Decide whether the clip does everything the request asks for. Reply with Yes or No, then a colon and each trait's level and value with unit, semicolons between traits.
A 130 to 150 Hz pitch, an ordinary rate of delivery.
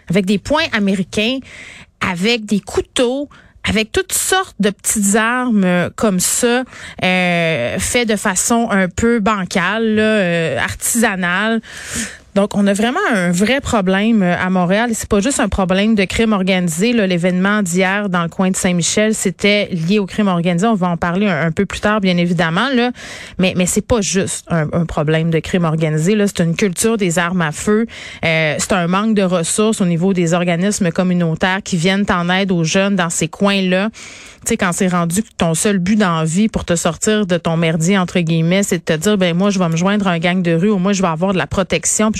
No: high, 195 Hz; average, 210 wpm